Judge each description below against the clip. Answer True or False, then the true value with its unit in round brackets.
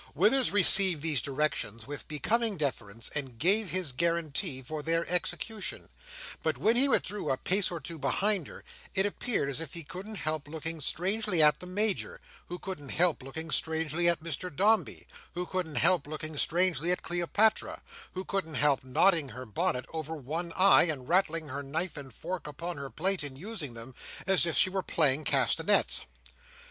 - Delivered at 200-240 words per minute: False (175 wpm)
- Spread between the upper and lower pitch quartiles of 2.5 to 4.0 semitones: False (4.4 semitones)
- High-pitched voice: False (165 Hz)